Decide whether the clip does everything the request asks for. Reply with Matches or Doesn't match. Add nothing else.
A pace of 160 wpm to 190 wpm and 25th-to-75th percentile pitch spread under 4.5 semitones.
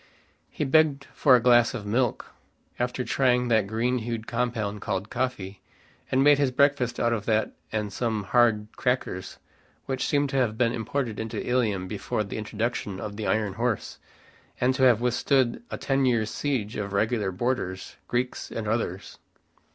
Matches